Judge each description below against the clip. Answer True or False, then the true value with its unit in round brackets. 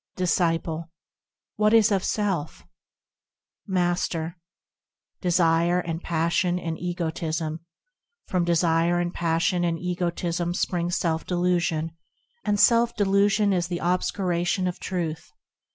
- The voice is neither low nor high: True (175 Hz)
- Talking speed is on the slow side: True (105 wpm)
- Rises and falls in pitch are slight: True (1.6 semitones)